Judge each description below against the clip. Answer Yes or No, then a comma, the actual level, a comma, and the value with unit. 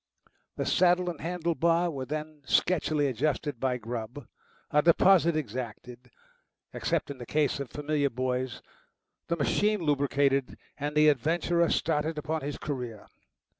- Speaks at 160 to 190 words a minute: No, slow, 135 wpm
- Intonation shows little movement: No, average, 3.9 semitones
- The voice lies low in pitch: No, medium, 150 Hz